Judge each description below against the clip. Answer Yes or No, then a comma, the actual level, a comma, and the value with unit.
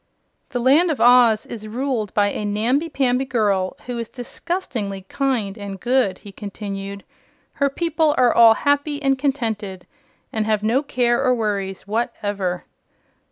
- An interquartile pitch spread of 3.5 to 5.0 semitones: Yes, average, 4.7 semitones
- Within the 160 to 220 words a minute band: No, average, 150 wpm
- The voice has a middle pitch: No, high, 230 Hz